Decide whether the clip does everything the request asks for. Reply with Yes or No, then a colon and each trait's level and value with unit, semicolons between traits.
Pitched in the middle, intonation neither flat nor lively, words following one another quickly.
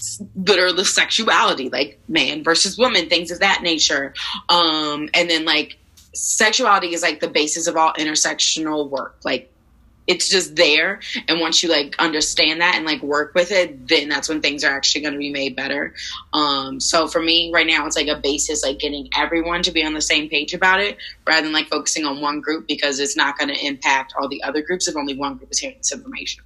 Yes: medium, 155 Hz; average, 3.0 semitones; fast, 220 wpm